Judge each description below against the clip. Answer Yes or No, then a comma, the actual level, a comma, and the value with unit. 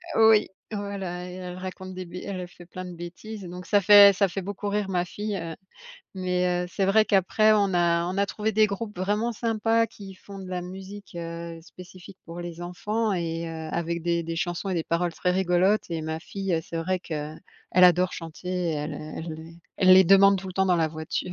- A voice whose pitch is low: No, medium, 180 Hz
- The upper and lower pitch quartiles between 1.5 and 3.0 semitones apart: Yes, average, 2.7 semitones